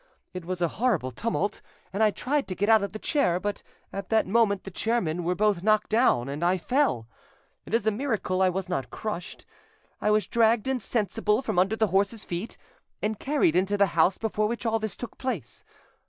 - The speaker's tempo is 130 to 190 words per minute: No, fast, 205 wpm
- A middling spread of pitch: Yes, average, 3.6 semitones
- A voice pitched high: Yes, high, 205 Hz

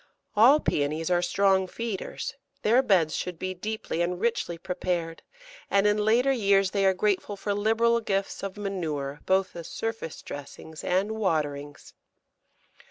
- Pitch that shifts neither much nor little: Yes, average, 3.7 semitones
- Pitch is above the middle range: Yes, high, 195 Hz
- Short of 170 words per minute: Yes, average, 145 wpm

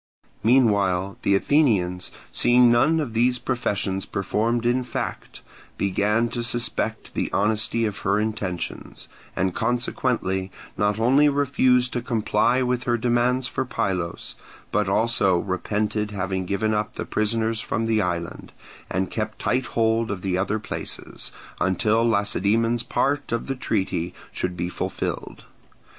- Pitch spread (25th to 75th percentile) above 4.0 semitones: No, average, 3.6 semitones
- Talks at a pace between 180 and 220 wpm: No, slow, 135 wpm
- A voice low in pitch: Yes, low, 110 Hz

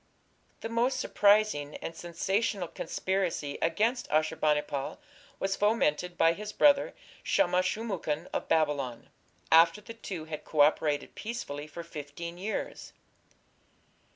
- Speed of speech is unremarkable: No, slow, 125 wpm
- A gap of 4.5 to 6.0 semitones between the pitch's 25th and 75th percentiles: Yes, wide, 5.5 semitones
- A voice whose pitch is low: No, medium, 170 Hz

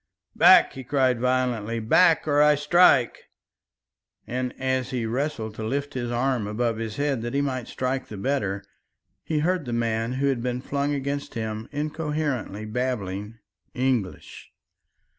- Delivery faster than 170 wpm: No, average, 150 wpm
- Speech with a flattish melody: No, average, 3.8 semitones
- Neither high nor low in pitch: No, low, 125 Hz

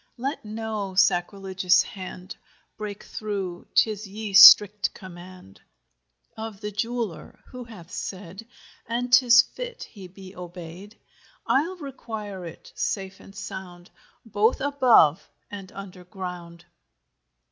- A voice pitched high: Yes, high, 200 Hz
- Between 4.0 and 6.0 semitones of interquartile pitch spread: No, average, 3.3 semitones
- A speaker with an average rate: No, slow, 110 wpm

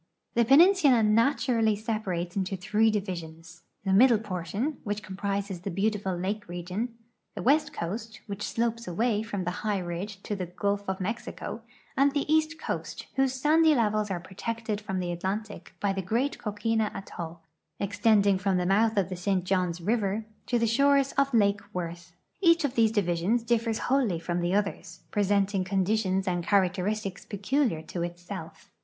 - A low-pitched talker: No, high, 205 Hz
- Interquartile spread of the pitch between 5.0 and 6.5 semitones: No, average, 3.6 semitones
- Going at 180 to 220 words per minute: No, average, 165 wpm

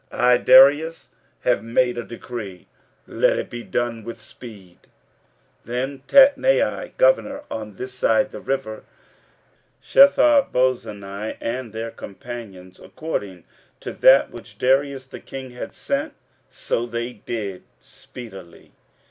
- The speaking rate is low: Yes, slow, 120 wpm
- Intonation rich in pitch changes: No, average, 3.6 semitones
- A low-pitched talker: Yes, low, 120 Hz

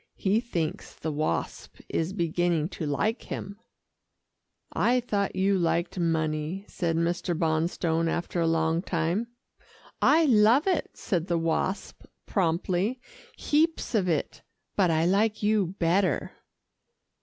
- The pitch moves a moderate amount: Yes, average, 3.9 semitones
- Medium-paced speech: No, slow, 125 wpm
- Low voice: No, medium, 175 Hz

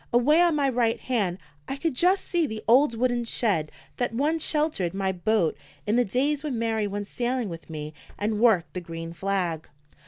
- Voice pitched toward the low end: No, high, 230 Hz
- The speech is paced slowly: No, average, 190 wpm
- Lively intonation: Yes, wide, 6.0 semitones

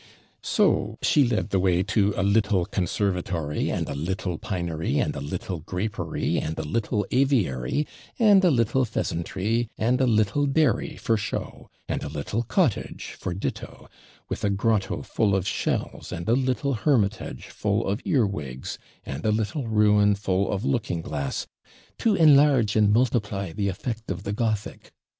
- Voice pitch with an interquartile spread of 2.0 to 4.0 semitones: No, average, 4.5 semitones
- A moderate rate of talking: Yes, average, 160 wpm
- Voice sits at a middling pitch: No, low, 105 Hz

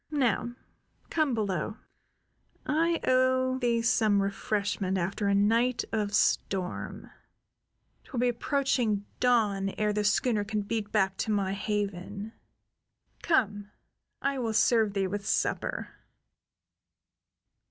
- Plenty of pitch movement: No, average, 3.6 semitones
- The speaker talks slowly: Yes, slow, 110 wpm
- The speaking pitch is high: Yes, high, 215 Hz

